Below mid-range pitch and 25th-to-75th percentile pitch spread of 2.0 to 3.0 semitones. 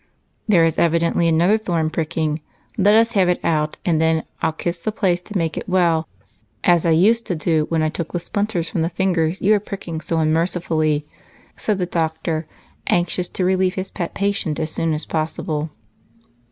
No: medium, 170 Hz; narrow, 2.6 semitones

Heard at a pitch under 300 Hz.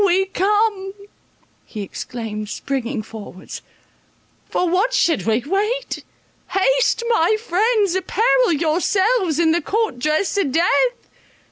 No: very high, 370 Hz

